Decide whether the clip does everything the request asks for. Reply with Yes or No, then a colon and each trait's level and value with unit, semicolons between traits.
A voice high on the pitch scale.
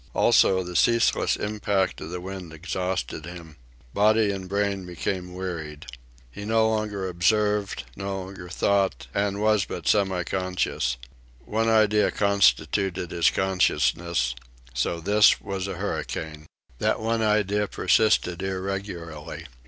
No: very low, 95 Hz